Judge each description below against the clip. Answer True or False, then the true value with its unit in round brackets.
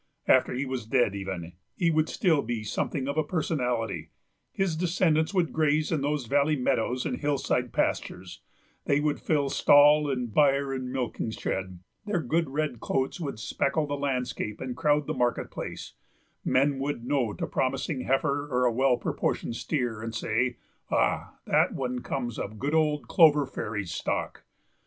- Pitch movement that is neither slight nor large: True (3.6 semitones)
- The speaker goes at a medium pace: True (165 wpm)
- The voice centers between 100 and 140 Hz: True (135 Hz)